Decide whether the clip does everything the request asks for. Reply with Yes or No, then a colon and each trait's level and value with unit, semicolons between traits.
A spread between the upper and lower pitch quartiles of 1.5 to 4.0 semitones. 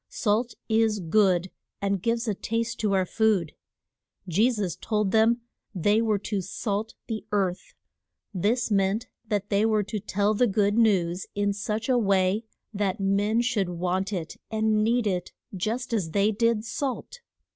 Yes: narrow, 2.5 semitones